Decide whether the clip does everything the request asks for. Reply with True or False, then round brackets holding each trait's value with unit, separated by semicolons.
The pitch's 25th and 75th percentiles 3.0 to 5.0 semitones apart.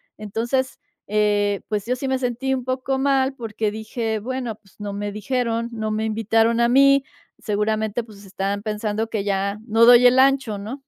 True (3.3 semitones)